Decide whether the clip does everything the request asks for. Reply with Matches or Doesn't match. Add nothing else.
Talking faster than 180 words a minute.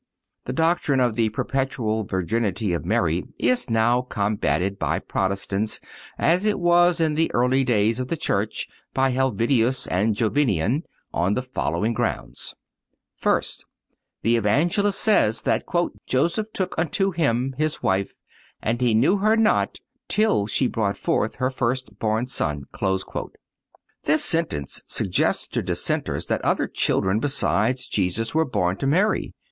Doesn't match